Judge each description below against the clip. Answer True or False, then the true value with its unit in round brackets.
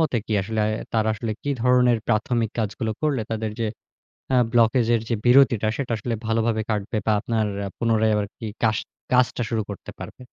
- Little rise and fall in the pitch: True (1.9 semitones)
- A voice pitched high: False (115 Hz)